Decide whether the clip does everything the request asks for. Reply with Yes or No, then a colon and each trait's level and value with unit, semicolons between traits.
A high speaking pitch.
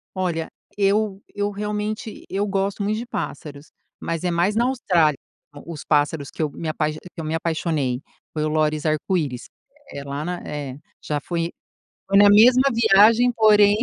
No: medium, 175 Hz